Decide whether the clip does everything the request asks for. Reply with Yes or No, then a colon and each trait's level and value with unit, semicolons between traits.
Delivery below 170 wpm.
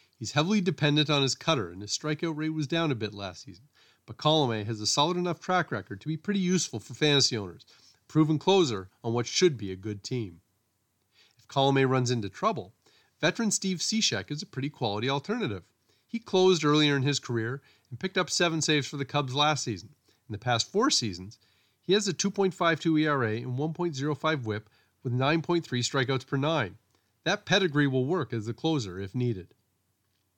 No: average, 190 wpm